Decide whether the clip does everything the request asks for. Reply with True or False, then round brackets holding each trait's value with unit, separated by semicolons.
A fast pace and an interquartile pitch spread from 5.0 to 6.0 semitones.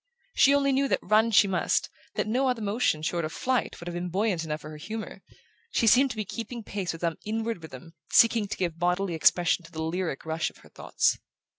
True (230 wpm; 5.5 semitones)